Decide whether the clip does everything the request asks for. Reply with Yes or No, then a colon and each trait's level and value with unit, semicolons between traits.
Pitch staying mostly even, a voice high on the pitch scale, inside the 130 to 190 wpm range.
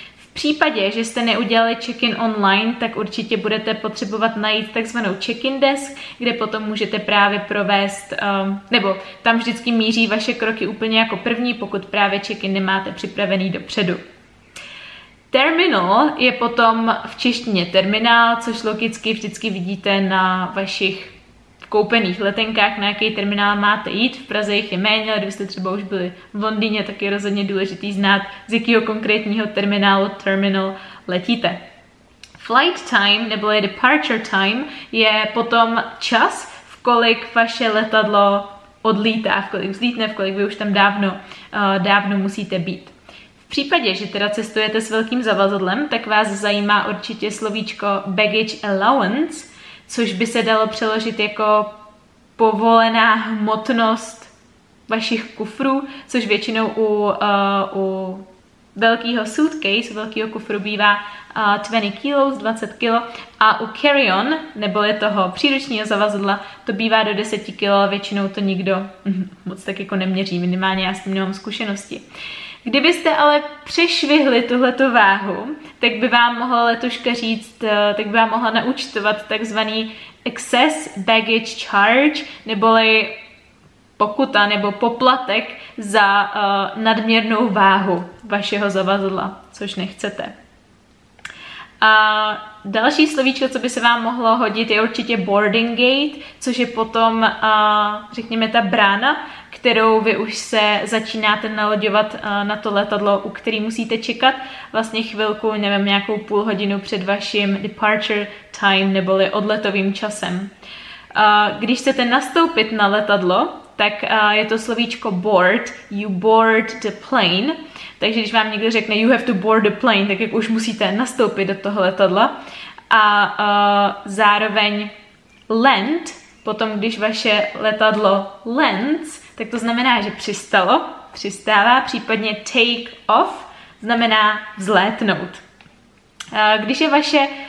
Yes: narrow, 2.3 semitones; high, 215 Hz; average, 135 wpm